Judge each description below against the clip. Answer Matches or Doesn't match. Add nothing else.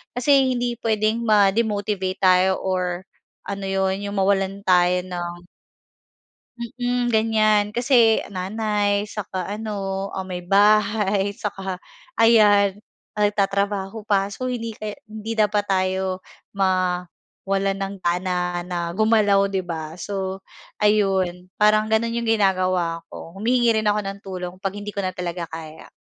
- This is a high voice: Matches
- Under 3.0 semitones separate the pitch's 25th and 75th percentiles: Matches